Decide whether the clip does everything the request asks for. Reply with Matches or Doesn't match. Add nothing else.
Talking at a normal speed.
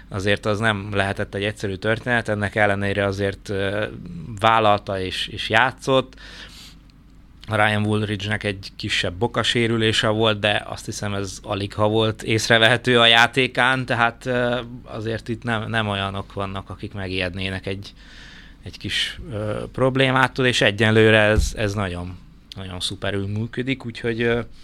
Matches